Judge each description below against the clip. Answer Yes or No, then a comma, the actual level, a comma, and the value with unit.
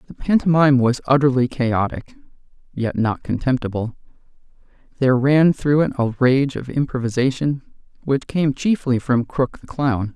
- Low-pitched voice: Yes, low, 130 Hz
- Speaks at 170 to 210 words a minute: No, slow, 135 wpm